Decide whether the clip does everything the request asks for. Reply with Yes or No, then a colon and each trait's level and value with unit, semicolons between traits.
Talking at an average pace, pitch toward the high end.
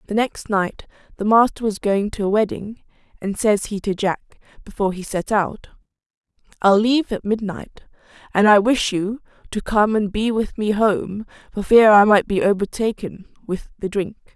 Yes: average, 180 wpm; high, 205 Hz